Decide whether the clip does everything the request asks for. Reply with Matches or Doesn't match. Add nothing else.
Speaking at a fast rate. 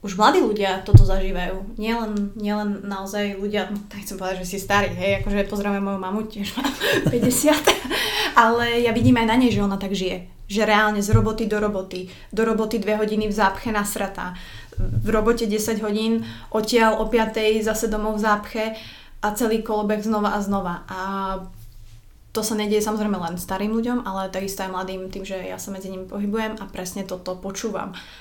Matches